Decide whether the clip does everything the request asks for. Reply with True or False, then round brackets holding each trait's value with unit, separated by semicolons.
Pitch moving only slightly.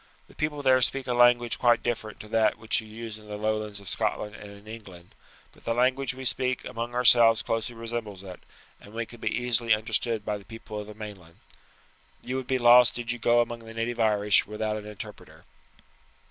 True (2.2 semitones)